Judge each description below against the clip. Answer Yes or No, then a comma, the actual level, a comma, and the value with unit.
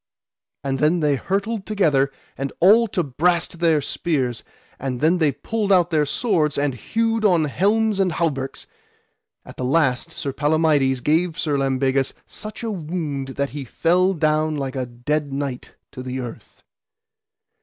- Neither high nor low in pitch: Yes, medium, 150 Hz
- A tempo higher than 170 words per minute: No, average, 155 wpm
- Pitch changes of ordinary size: Yes, average, 4.7 semitones